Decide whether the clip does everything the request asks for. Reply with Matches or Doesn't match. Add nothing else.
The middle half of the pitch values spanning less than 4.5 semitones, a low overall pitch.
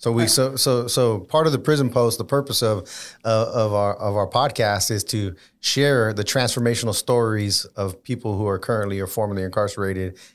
Matches